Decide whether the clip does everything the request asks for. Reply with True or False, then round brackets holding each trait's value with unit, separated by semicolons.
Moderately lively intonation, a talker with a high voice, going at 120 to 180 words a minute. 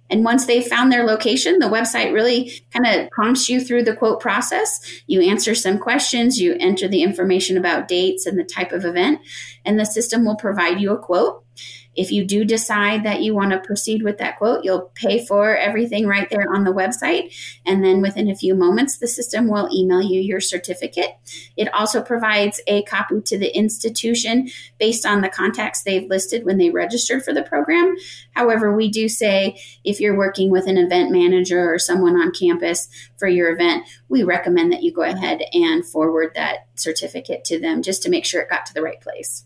False (4.3 semitones; 205 Hz; 205 wpm)